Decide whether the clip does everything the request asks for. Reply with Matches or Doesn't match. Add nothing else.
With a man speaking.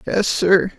Matches